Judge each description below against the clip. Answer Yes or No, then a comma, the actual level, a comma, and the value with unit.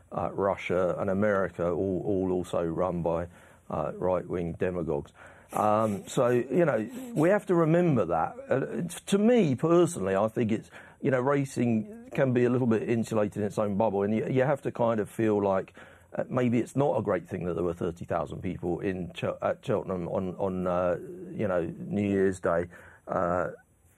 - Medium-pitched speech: No, low, 110 Hz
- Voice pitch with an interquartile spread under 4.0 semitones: No, average, 5.2 semitones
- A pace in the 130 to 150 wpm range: No, average, 190 wpm